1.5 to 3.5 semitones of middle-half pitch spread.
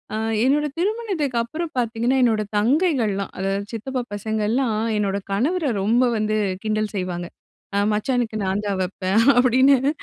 No: average, 4.5 semitones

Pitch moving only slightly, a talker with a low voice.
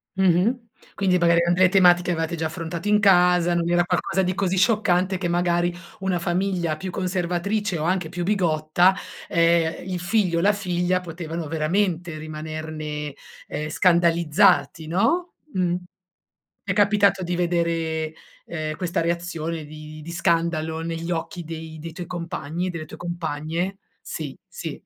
No: narrow, 2.2 semitones; medium, 175 Hz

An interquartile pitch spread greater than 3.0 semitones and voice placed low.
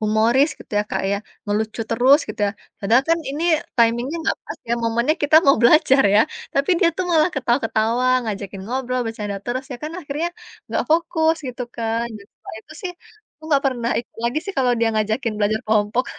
No: average, 4.4 semitones; high, 245 Hz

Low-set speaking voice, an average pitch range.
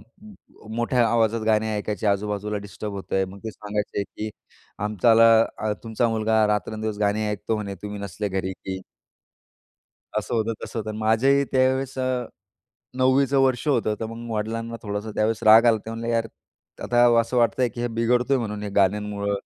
No: low, 110 Hz; narrow, 2.1 semitones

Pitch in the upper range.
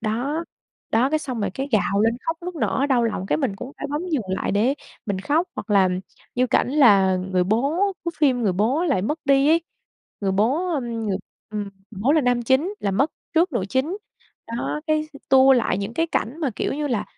Yes: very high, 250 Hz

